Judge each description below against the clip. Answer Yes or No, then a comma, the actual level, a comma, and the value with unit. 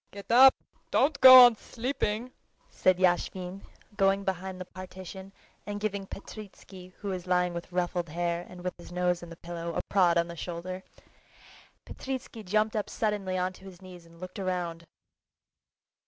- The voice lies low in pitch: No, medium, 185 Hz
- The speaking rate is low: No, average, 160 wpm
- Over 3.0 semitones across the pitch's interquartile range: No, narrow, 2.6 semitones